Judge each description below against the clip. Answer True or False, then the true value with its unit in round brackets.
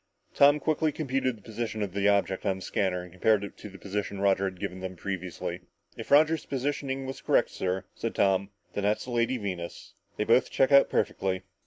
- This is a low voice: True (100 Hz)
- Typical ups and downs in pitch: False (5.7 semitones)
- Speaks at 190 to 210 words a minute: True (205 wpm)